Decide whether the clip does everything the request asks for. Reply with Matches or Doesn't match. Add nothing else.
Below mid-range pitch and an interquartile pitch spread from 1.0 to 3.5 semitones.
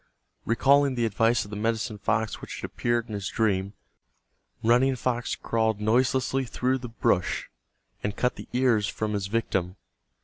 Matches